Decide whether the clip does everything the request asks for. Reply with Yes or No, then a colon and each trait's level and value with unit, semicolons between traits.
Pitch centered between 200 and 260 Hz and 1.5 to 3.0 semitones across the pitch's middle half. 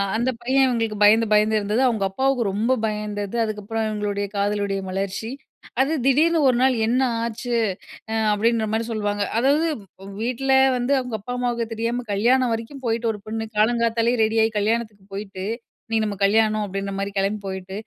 Yes: high, 220 Hz; narrow, 2.6 semitones